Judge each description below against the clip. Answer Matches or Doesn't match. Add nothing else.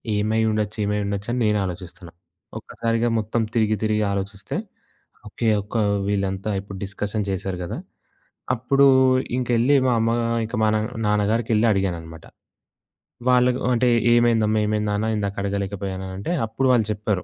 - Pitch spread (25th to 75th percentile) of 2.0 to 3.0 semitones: Matches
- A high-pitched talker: Doesn't match